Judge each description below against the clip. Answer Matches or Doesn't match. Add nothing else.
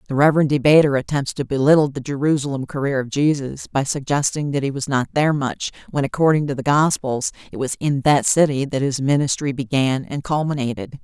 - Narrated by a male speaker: Doesn't match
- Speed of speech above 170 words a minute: Matches